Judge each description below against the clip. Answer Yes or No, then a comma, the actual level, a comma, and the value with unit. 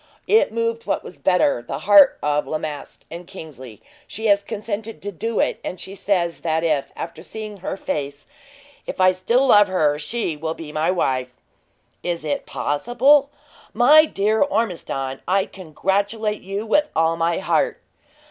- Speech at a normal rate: Yes, average, 160 wpm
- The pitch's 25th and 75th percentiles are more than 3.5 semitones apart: Yes, wide, 5.6 semitones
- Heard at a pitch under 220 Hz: Yes, medium, 185 Hz